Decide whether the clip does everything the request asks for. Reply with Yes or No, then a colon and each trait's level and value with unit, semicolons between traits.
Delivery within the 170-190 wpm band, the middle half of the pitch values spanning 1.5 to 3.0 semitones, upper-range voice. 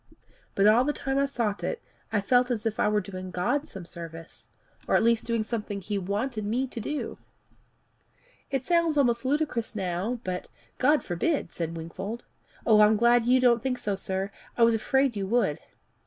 No: average, 185 wpm; average, 4.3 semitones; high, 225 Hz